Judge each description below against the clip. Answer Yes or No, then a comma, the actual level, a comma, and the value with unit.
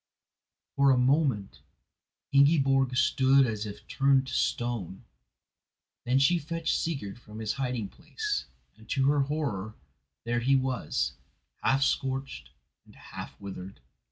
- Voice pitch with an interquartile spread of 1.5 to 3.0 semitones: No, average, 4.0 semitones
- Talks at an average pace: No, slow, 130 wpm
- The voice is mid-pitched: No, low, 130 Hz